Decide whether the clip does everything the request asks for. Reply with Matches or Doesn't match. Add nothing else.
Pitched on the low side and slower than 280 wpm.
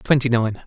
Matches